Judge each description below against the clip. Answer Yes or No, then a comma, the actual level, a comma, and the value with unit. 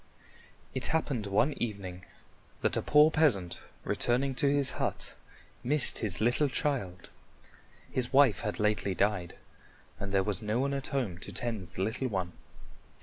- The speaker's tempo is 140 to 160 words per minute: Yes, average, 150 wpm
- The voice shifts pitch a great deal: Yes, wide, 5.8 semitones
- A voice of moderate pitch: No, low, 115 Hz